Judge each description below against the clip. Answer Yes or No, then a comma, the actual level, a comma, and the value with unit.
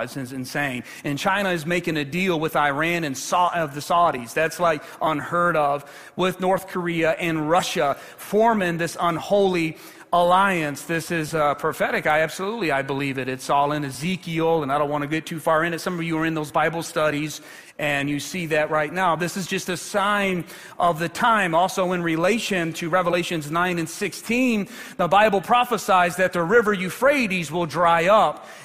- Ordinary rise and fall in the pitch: Yes, average, 3.2 semitones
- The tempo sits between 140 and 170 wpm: No, average, 195 wpm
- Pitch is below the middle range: No, medium, 170 Hz